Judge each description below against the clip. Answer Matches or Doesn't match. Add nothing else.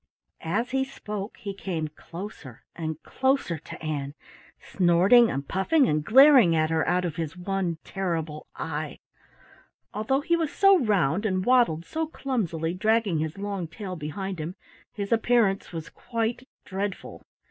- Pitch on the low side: Doesn't match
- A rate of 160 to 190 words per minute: Doesn't match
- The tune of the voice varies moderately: Doesn't match